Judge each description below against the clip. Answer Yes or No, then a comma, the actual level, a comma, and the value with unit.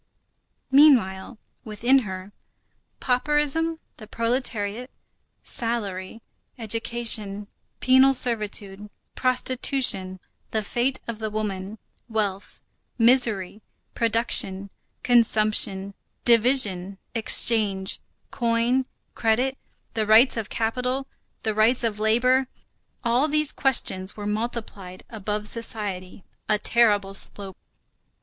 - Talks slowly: Yes, slow, 85 wpm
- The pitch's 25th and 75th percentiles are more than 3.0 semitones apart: Yes, average, 3.4 semitones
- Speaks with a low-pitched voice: No, high, 225 Hz